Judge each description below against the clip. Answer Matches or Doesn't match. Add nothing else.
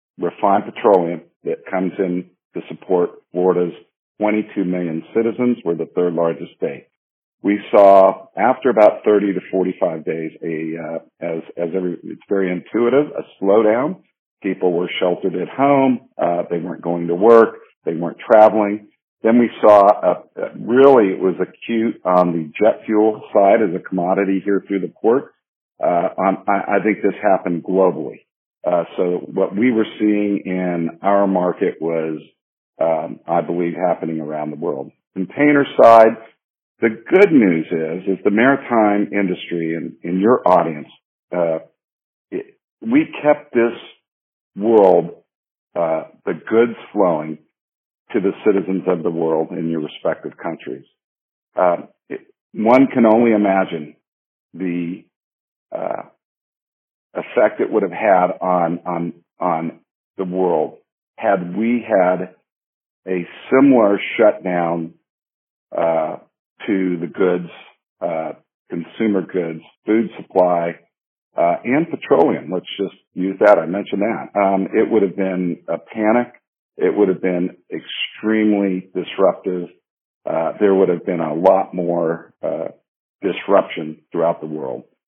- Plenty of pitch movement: Doesn't match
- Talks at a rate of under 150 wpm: Matches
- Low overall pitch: Matches